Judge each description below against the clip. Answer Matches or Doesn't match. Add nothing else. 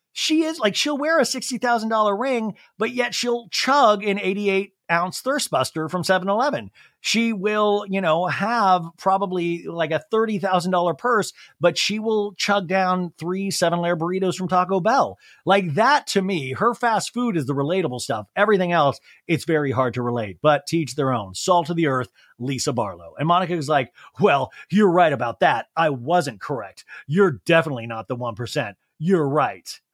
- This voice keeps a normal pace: Matches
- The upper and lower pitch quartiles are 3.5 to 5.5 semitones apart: Matches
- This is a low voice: Doesn't match